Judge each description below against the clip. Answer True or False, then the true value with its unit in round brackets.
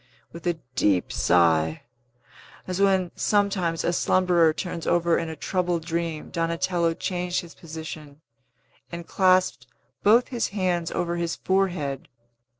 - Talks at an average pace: False (130 wpm)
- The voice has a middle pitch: True (170 Hz)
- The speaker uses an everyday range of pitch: False (2.1 semitones)